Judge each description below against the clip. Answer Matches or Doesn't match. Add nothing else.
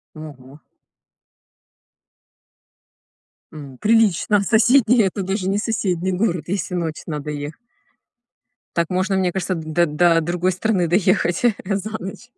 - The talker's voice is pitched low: Doesn't match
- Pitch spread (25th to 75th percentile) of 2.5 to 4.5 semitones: Matches